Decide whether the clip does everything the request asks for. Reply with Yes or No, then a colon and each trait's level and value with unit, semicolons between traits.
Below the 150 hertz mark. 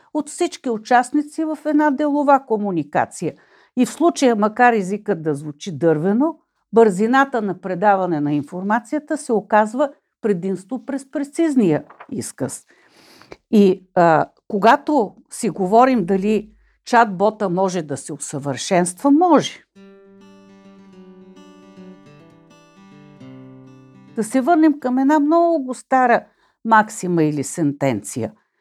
No: high, 210 Hz